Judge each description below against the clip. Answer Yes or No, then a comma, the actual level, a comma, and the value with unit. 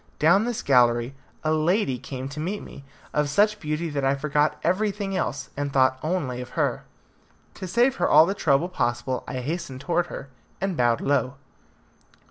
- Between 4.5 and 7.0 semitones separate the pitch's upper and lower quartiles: Yes, wide, 5.4 semitones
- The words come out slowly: No, average, 175 wpm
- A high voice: No, medium, 150 Hz